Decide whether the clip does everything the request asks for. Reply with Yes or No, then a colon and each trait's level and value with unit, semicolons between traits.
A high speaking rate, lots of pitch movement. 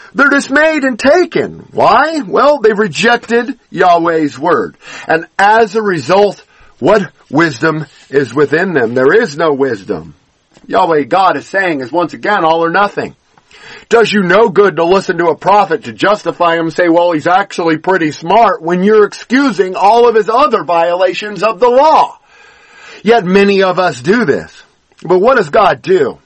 No: average, 170 wpm; wide, 5.7 semitones